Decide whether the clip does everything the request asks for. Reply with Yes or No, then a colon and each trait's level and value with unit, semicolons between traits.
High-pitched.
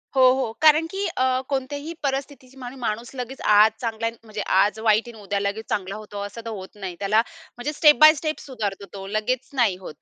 Yes: high, 230 Hz